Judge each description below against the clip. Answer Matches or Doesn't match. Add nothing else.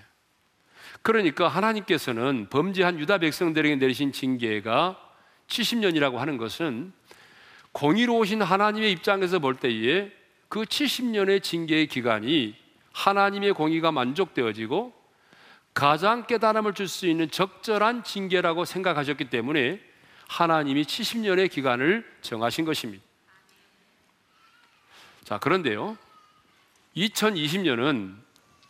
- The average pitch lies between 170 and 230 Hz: Matches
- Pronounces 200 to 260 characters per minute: Matches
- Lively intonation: Matches